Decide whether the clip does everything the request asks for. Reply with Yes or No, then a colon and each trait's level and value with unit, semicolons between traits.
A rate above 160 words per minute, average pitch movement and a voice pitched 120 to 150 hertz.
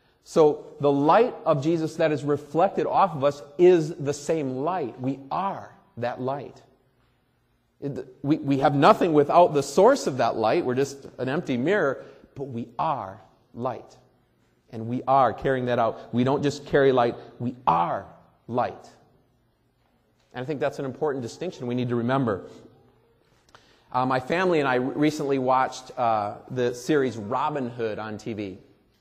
No: average, 155 wpm; average, 3.1 semitones; low, 135 Hz